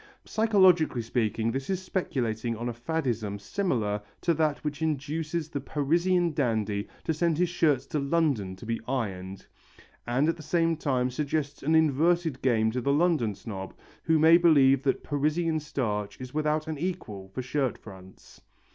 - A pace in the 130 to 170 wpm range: Yes, average, 165 wpm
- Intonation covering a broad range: Yes, wide, 5.7 semitones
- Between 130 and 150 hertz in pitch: Yes, medium, 140 Hz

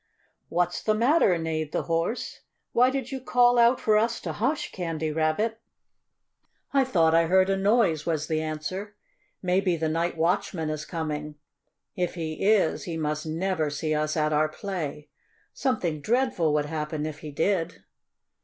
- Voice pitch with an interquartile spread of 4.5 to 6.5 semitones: Yes, average, 5.0 semitones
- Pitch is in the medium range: Yes, medium, 165 Hz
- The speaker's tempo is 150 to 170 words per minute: Yes, average, 165 wpm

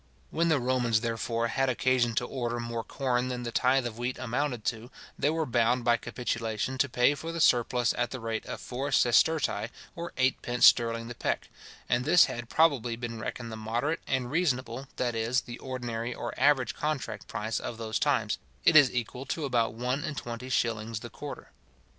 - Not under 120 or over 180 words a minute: No, average, 190 wpm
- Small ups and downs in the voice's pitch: Yes, narrow, 2.2 semitones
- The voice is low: Yes, low, 120 Hz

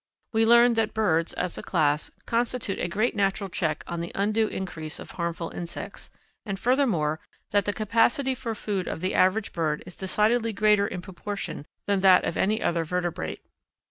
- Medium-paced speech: Yes, average, 175 wpm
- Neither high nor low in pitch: No, high, 195 Hz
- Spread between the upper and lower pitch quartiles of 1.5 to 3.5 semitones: No, average, 4.3 semitones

